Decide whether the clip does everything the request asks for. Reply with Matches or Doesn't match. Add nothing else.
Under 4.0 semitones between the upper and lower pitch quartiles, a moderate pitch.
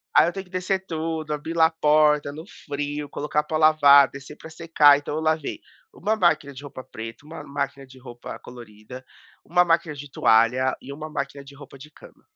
Matches